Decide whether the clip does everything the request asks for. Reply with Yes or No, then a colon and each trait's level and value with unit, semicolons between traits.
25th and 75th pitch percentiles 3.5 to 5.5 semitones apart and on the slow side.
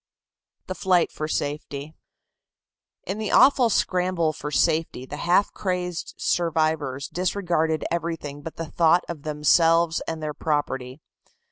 No: average, 2.9 semitones; slow, 125 wpm